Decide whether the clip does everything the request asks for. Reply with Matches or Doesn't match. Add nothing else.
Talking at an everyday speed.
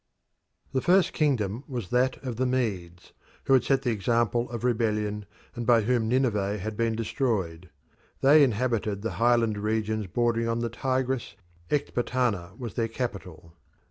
Matches